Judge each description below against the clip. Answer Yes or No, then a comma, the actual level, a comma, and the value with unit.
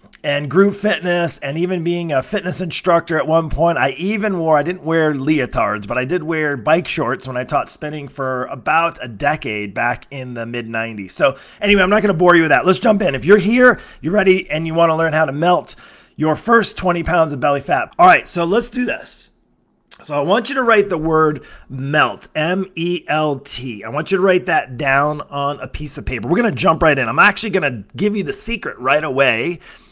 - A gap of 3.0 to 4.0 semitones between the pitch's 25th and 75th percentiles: No, average, 4.7 semitones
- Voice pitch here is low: No, medium, 165 Hz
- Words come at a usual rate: No, fast, 230 wpm